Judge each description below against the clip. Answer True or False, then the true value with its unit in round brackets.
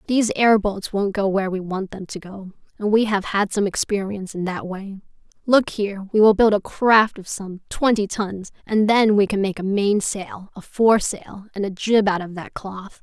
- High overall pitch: True (200 Hz)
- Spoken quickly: True (215 wpm)